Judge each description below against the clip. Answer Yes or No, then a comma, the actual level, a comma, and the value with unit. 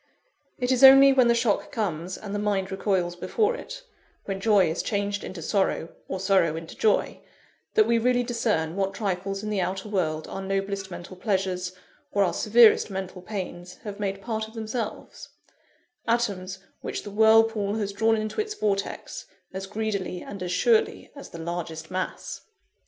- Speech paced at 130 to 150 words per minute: No, average, 170 wpm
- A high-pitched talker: Yes, high, 200 Hz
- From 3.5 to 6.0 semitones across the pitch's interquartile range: No, average, 3.1 semitones